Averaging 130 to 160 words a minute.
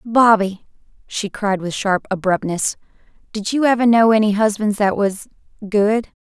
Yes: slow, 135 wpm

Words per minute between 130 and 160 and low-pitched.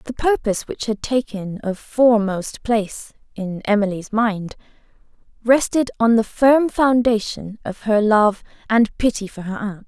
No: average, 145 wpm; high, 220 Hz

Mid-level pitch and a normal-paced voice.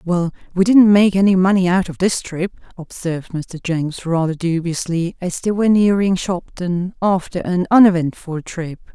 Yes: medium, 180 Hz; average, 160 wpm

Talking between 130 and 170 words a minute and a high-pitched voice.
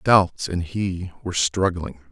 No: average, 140 wpm; very low, 90 Hz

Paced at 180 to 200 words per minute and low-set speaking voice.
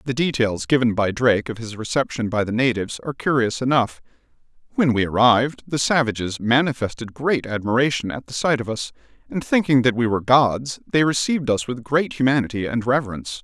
Yes: average, 185 wpm; low, 125 Hz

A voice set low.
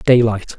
Yes: low, 110 Hz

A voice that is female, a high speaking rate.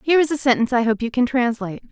Yes: female; fast, 280 wpm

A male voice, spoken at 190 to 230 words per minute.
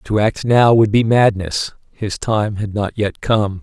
Yes: male; average, 200 wpm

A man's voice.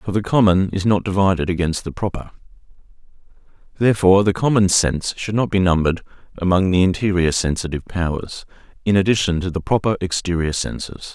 Yes: male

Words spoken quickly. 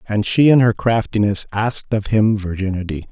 No: average, 175 wpm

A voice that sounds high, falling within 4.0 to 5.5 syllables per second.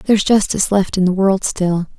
Yes: high, 195 Hz; 5.4 syllables/s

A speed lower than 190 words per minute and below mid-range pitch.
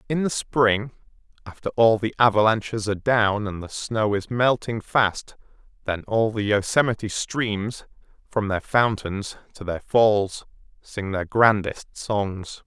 Yes: average, 140 wpm; low, 105 Hz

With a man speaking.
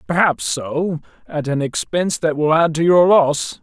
Yes: male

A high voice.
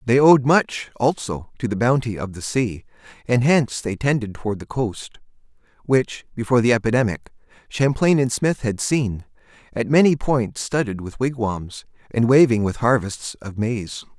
No: low, 120 Hz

